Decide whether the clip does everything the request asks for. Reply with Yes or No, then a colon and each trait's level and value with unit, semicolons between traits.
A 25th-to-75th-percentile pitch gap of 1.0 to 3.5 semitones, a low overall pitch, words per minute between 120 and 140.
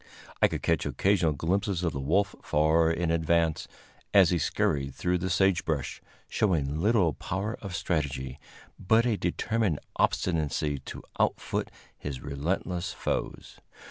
No: average, 4.2 semitones; very low, 85 Hz; slow, 135 wpm